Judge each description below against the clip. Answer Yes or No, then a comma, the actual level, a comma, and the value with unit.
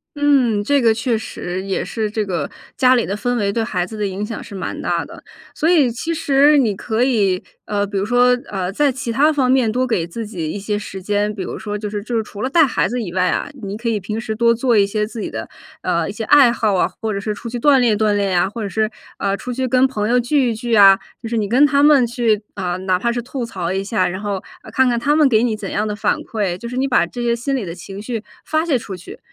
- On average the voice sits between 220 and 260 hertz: Yes, high, 225 Hz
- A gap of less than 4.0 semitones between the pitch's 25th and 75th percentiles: Yes, average, 3.6 semitones